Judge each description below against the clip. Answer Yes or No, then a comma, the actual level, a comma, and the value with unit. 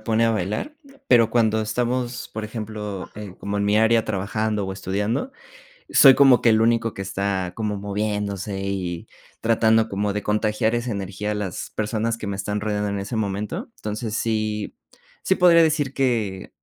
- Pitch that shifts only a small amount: Yes, narrow, 2.2 semitones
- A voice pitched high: No, low, 105 Hz